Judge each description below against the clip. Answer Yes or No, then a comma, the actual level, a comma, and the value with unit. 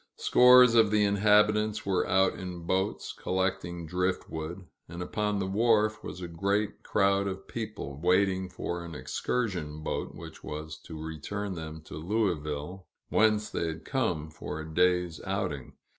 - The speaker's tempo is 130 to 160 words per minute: Yes, average, 150 wpm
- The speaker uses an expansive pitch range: No, average, 4.2 semitones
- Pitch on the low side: Yes, very low, 95 Hz